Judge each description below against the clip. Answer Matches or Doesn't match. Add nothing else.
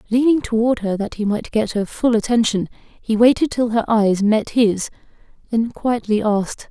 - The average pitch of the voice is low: Doesn't match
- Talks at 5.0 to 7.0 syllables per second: Doesn't match